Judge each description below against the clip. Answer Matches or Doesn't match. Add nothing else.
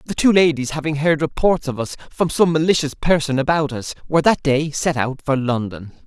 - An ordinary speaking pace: Doesn't match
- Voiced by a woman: Doesn't match